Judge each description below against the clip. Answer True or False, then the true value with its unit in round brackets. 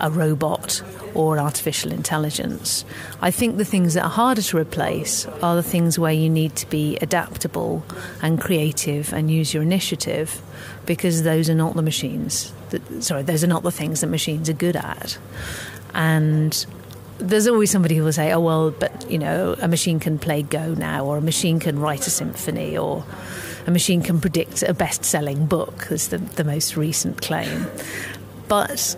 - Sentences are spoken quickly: False (180 wpm)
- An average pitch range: False (2.2 semitones)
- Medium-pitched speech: True (160 Hz)